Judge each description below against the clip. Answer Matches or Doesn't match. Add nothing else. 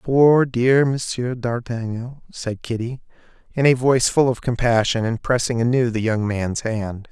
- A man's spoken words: Matches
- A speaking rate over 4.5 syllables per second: Doesn't match